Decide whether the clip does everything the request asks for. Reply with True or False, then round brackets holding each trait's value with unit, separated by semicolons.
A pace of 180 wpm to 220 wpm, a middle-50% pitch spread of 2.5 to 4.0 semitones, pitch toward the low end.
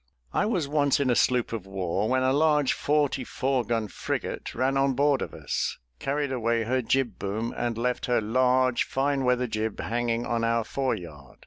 True (190 wpm; 2.9 semitones; 125 Hz)